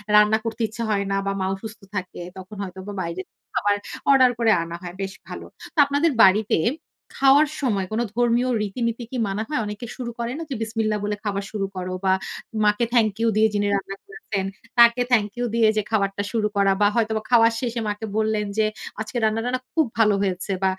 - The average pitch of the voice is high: Yes, high, 215 Hz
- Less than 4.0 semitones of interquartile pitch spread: Yes, average, 2.9 semitones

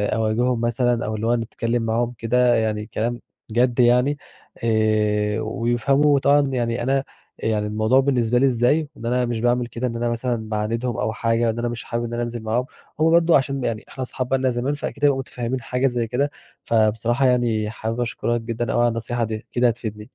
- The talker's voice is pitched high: No, low, 120 Hz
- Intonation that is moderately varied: No, narrow, 1.9 semitones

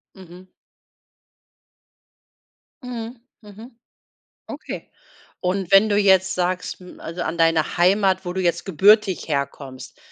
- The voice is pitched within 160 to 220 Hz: Yes, medium, 185 Hz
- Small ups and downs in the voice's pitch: No, average, 3.0 semitones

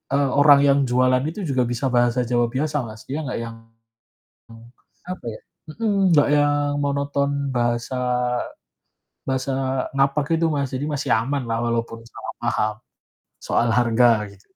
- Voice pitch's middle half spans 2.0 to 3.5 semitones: Yes, average, 3.2 semitones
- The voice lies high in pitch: No, low, 130 Hz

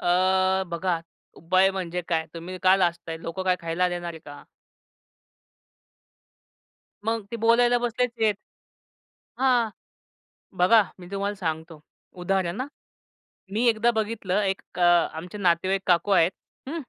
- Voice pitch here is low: No, medium, 185 Hz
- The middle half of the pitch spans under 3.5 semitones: No, average, 3.8 semitones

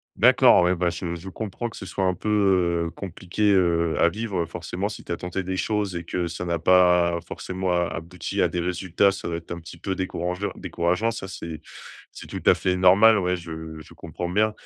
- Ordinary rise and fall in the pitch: No, narrow, 2.0 semitones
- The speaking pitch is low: Yes, very low, 90 Hz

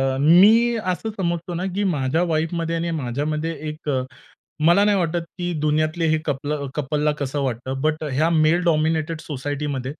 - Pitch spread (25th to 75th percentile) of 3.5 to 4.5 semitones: No, average, 2.9 semitones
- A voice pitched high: No, medium, 155 Hz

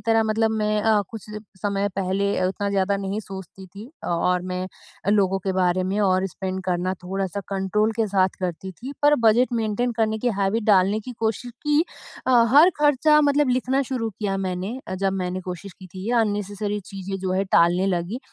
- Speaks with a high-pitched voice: Yes, high, 200 Hz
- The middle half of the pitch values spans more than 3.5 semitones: No, average, 3.0 semitones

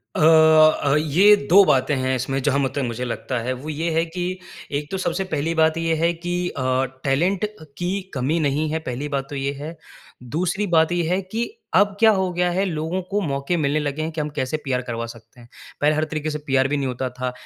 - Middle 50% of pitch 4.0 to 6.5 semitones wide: Yes, average, 4.4 semitones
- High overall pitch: No, medium, 155 Hz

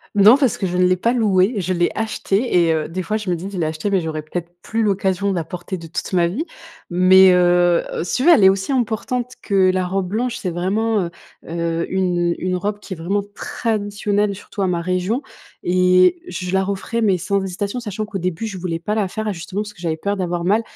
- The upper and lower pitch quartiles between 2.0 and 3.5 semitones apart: Yes, average, 2.9 semitones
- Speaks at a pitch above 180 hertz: Yes, high, 190 Hz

